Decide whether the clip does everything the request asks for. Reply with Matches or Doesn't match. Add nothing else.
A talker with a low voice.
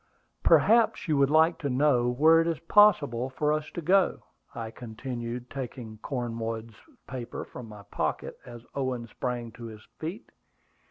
Matches